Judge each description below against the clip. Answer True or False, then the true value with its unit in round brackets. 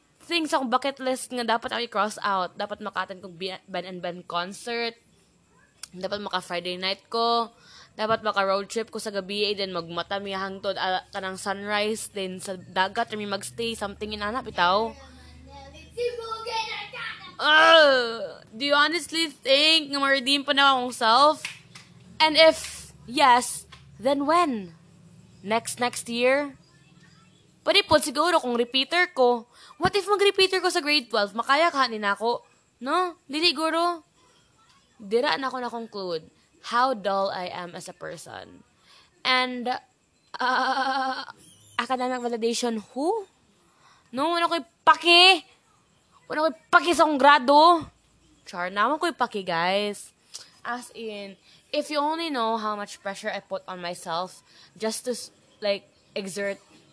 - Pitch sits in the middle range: False (235 Hz)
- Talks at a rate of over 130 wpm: True (140 wpm)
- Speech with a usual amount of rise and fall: False (6.9 semitones)